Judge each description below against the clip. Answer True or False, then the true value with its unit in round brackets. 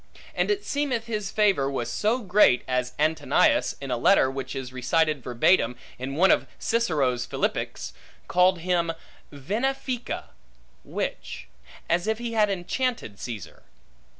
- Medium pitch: True (175 Hz)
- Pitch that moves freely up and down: True (8.8 semitones)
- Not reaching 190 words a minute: True (135 wpm)